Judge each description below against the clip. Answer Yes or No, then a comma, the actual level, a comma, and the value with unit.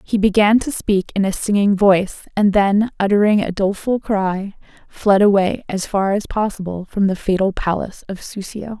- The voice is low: No, high, 200 Hz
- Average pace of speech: Yes, average, 175 wpm